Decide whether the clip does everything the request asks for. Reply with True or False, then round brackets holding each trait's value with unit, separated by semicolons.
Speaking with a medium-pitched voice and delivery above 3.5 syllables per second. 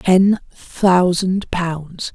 False (180 Hz; 2.0 syllables/s)